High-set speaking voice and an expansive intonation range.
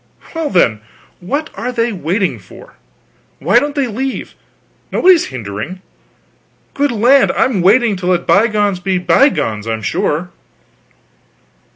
Yes: high, 200 Hz; wide, 6.7 semitones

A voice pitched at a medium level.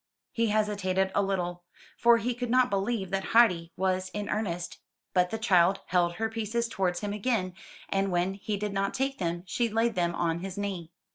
No: high, 195 Hz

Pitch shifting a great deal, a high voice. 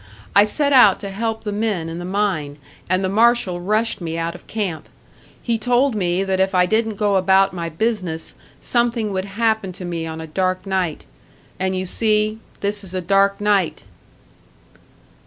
No: average, 3.2 semitones; high, 195 Hz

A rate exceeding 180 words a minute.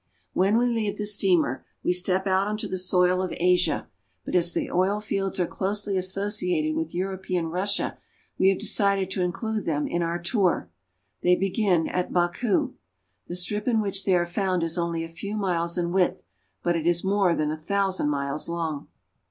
Yes: average, 190 wpm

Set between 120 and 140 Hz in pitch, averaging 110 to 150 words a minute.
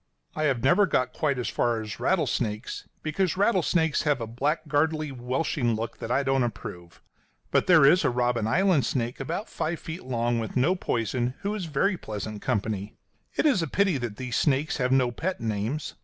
No: low, 135 Hz; average, 185 wpm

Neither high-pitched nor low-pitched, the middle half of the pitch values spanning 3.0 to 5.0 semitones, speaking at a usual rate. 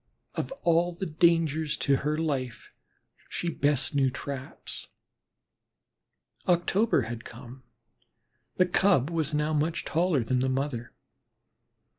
No: medium, 150 Hz; average, 4.2 semitones; slow, 115 wpm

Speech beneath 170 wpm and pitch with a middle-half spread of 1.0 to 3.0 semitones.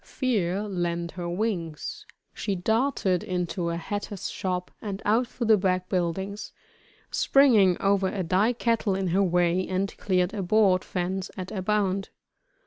Yes: average, 150 wpm; average, 2.7 semitones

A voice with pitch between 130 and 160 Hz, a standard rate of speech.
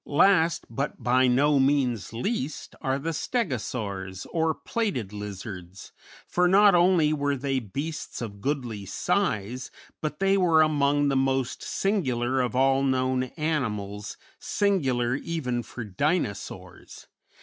No: low, 135 Hz; slow, 125 wpm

